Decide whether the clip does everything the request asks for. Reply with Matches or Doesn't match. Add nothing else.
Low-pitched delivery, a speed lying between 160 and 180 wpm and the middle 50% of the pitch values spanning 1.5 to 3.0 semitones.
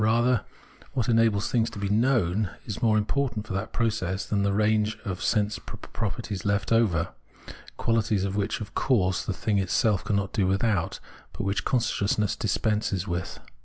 Matches